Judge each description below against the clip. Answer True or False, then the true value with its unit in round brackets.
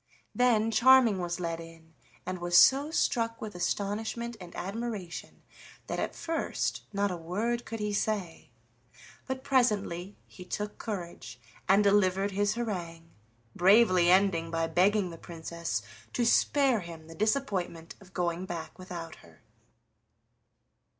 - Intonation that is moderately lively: True (4.5 semitones)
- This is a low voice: False (195 Hz)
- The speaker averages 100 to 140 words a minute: True (135 wpm)